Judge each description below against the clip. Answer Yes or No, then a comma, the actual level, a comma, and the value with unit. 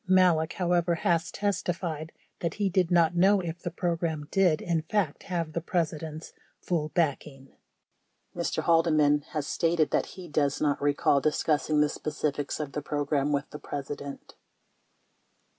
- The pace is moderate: Yes, average, 155 wpm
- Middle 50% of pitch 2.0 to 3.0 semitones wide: Yes, average, 2.7 semitones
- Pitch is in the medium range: Yes, medium, 160 Hz